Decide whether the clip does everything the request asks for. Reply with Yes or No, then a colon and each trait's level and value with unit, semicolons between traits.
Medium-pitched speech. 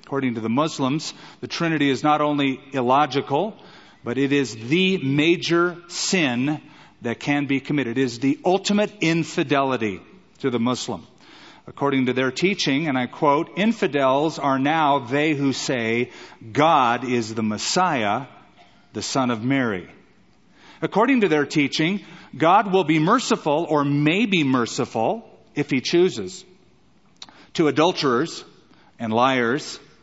Yes: medium, 145 Hz